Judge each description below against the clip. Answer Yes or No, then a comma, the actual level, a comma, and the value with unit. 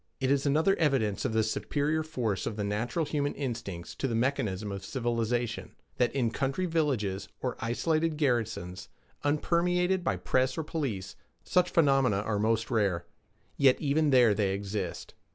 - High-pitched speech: No, low, 125 Hz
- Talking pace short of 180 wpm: Yes, average, 155 wpm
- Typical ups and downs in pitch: No, wide, 5.7 semitones